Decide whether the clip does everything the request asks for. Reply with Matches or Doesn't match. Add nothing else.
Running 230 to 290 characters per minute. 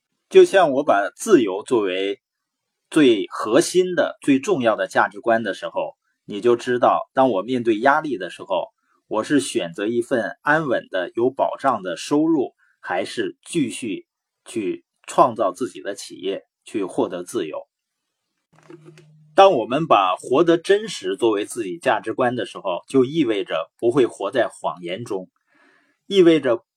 Doesn't match